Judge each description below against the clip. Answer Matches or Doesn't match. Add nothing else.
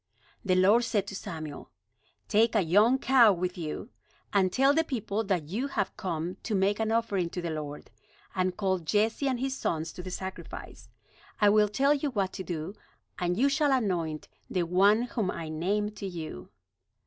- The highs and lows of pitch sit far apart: Doesn't match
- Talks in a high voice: Matches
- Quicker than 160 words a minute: Matches